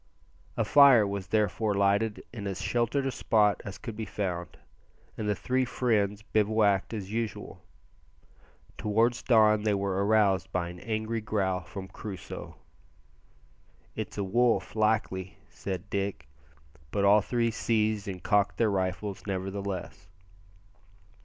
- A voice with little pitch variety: Yes, narrow, 2.2 semitones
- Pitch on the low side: Yes, low, 105 Hz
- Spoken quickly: No, slow, 135 wpm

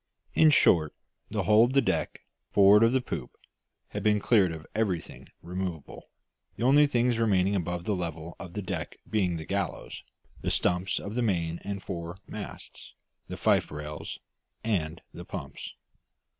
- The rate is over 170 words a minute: No, average, 160 wpm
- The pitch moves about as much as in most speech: Yes, average, 4.5 semitones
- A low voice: Yes, very low, 95 Hz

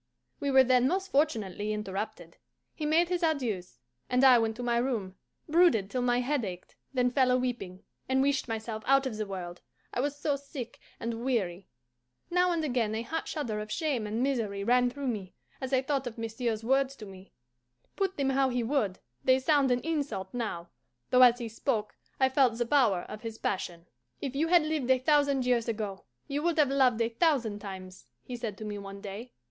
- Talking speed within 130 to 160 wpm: No, fast, 205 wpm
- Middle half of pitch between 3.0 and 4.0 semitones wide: No, average, 4.4 semitones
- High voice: Yes, high, 245 Hz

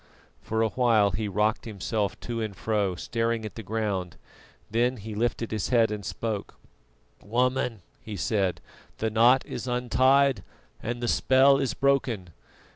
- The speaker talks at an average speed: Yes, average, 150 wpm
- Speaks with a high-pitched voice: No, low, 110 Hz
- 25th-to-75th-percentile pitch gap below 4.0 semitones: Yes, average, 2.9 semitones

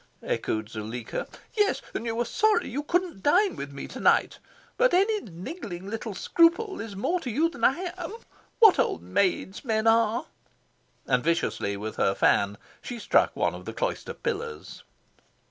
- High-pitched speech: Yes, high, 230 Hz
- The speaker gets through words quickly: No, average, 165 wpm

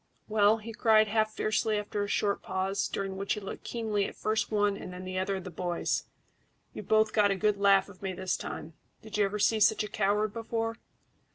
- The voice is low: No, high, 205 Hz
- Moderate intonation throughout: No, narrow, 1.9 semitones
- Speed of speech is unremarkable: No, fast, 215 wpm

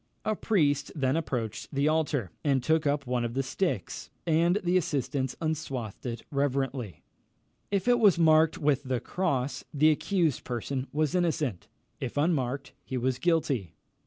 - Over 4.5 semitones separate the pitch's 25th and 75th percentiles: No, average, 3.8 semitones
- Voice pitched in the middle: Yes, medium, 145 Hz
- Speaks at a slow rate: No, average, 155 wpm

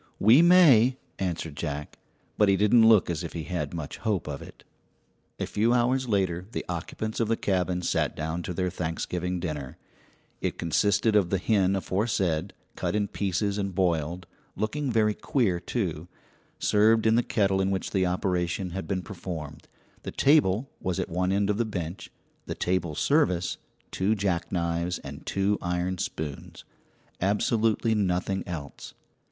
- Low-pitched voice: Yes, very low, 95 Hz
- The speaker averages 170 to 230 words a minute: No, average, 160 wpm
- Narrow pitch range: No, average, 3.6 semitones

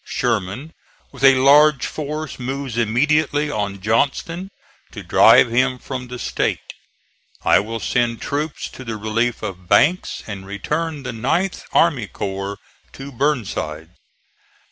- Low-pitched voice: Yes, low, 125 Hz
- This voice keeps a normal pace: No, slow, 130 wpm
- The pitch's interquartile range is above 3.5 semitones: Yes, average, 5.3 semitones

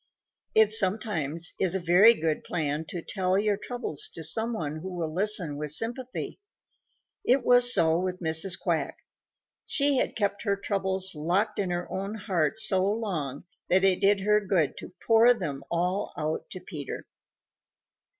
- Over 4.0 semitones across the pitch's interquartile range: Yes, average, 4.5 semitones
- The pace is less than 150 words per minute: No, average, 160 wpm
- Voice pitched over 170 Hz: Yes, high, 190 Hz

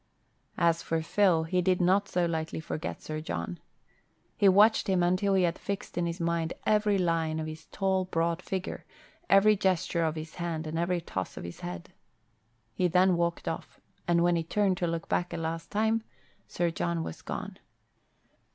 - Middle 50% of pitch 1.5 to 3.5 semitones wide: Yes, narrow, 2.5 semitones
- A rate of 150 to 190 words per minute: Yes, average, 185 wpm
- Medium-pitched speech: Yes, medium, 170 Hz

